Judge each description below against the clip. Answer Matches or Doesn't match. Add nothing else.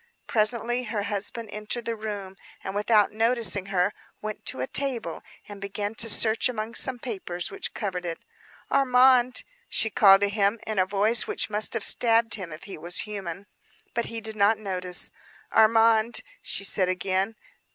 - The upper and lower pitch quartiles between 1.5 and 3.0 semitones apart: Matches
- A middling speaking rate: Matches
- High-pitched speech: Matches